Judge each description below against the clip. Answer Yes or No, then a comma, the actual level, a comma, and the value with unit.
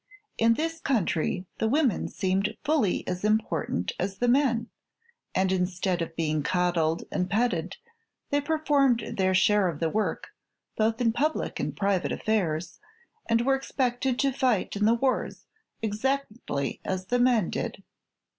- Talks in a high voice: Yes, high, 215 Hz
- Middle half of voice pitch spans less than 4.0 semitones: No, wide, 5.5 semitones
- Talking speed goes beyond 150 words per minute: No, average, 145 wpm